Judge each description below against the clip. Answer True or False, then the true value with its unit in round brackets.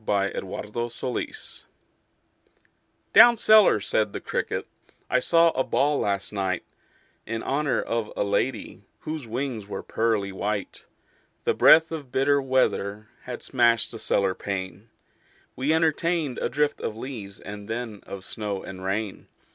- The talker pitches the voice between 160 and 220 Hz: False (115 Hz)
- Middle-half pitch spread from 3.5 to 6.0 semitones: True (5.3 semitones)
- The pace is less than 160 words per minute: True (140 wpm)